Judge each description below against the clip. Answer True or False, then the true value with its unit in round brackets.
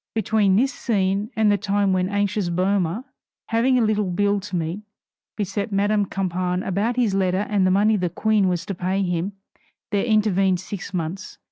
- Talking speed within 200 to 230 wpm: False (180 wpm)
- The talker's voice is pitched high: True (200 Hz)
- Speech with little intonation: True (2.3 semitones)